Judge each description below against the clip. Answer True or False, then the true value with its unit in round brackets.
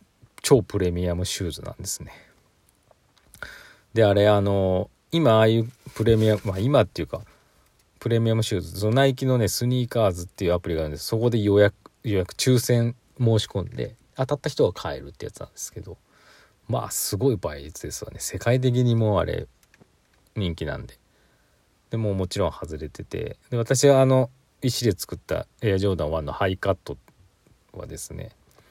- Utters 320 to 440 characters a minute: True (345 characters per minute)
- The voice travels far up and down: False (4.3 semitones)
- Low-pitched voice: True (110 Hz)